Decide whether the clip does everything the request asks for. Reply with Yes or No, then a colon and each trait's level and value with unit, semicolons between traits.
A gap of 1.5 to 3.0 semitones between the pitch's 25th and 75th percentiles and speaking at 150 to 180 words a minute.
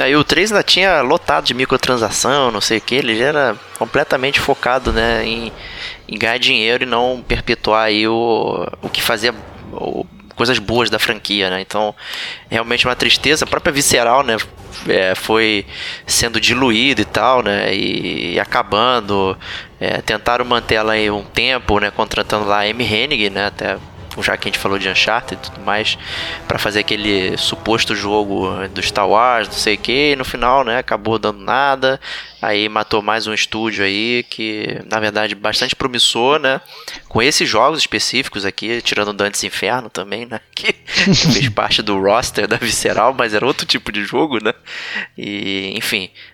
Yes: average, 2.7 semitones; average, 175 wpm